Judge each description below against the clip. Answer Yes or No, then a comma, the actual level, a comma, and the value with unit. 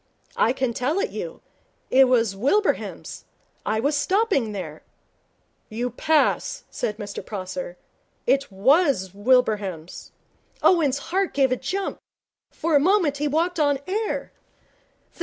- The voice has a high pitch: Yes, very high, 270 Hz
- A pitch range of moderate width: No, wide, 7.6 semitones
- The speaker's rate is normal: No, slow, 125 wpm